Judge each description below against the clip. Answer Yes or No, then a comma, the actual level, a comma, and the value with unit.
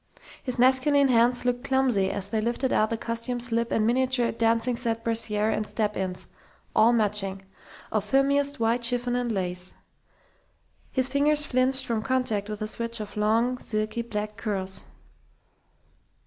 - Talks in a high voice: Yes, high, 230 Hz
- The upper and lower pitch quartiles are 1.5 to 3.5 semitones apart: Yes, average, 3.0 semitones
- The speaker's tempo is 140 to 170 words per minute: Yes, average, 150 wpm